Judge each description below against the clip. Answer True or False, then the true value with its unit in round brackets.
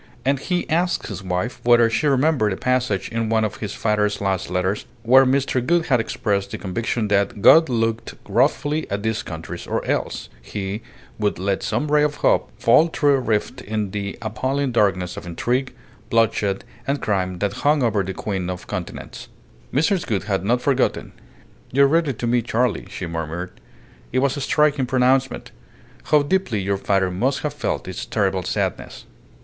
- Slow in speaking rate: False (180 wpm)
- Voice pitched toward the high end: False (115 Hz)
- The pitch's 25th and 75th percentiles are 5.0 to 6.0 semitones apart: True (5.3 semitones)